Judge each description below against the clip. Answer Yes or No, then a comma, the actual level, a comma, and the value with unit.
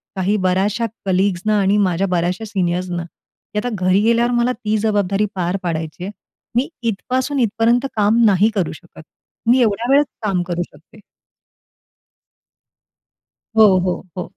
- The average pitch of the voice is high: Yes, high, 200 Hz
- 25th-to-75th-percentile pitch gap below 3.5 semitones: No, average, 3.8 semitones